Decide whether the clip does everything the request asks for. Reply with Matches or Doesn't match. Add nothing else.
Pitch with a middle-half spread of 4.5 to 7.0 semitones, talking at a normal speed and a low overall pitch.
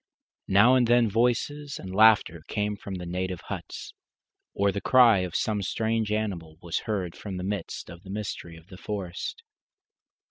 Doesn't match